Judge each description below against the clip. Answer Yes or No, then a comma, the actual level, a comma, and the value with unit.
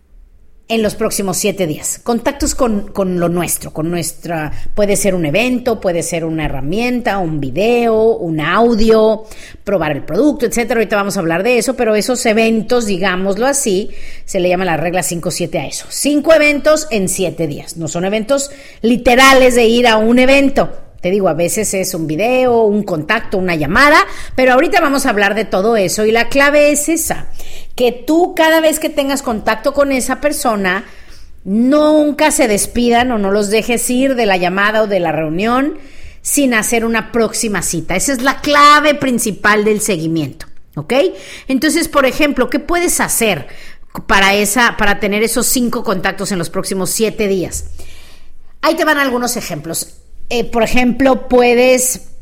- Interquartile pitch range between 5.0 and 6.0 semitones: Yes, wide, 5.4 semitones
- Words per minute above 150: Yes, average, 170 wpm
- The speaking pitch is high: Yes, high, 220 Hz